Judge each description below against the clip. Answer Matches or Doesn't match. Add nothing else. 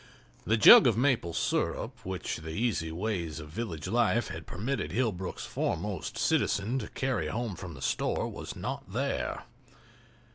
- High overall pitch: Doesn't match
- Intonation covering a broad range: Matches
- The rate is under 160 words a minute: Matches